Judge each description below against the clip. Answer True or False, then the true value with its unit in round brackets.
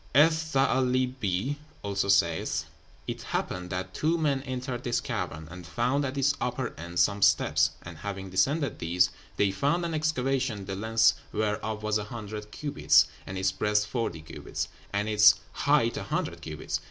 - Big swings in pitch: True (5.7 semitones)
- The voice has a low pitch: True (110 Hz)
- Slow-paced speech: False (165 wpm)